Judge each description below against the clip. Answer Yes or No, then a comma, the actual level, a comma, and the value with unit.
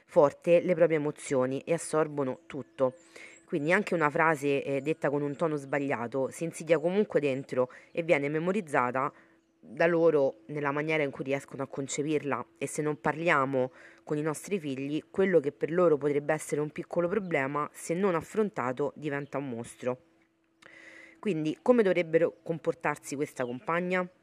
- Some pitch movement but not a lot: Yes, average, 3.3 semitones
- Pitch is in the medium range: Yes, medium, 150 Hz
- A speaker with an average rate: Yes, average, 155 wpm